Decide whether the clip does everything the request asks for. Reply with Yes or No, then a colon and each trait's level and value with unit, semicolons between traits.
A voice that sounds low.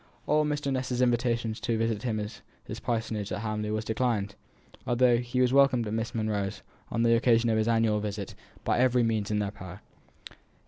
Yes: low, 115 Hz